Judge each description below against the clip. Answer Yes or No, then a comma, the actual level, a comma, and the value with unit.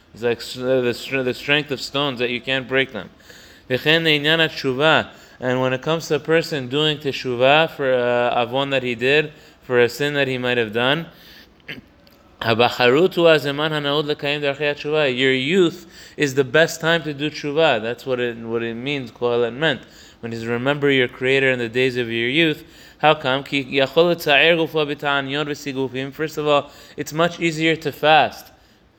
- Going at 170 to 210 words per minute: No, average, 155 wpm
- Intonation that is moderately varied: Yes, average, 3.3 semitones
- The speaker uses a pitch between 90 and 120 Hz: No, medium, 140 Hz